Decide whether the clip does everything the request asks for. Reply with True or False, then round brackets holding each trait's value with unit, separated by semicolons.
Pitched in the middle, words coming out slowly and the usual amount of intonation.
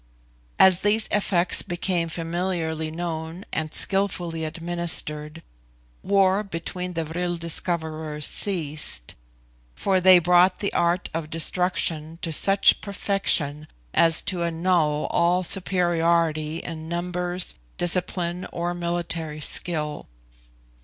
False (170 Hz; 105 wpm; 2.1 semitones)